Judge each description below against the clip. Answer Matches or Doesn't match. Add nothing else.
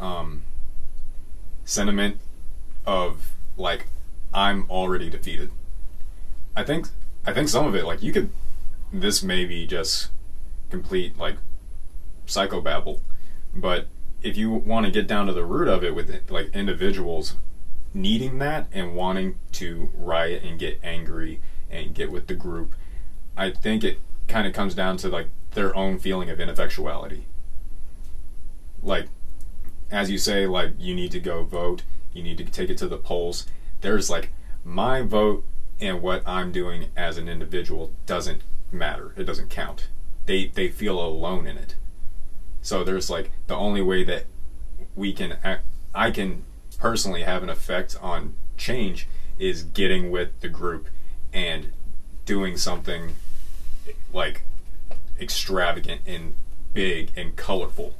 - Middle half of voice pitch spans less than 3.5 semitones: Doesn't match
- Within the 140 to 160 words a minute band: Matches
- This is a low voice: Matches